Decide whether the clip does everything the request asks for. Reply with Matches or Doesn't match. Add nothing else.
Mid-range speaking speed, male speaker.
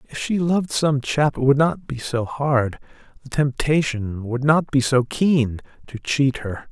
Matches